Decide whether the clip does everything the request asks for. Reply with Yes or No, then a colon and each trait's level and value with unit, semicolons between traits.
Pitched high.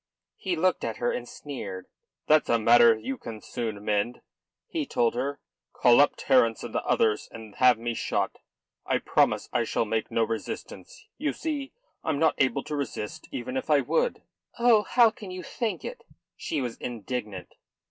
No: low, 125 Hz